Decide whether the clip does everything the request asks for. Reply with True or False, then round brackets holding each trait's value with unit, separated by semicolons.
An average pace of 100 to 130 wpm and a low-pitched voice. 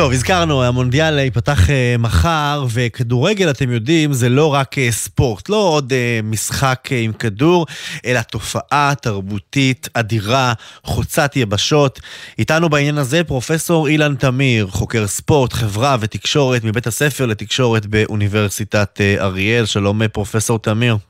True (115 wpm; 125 Hz)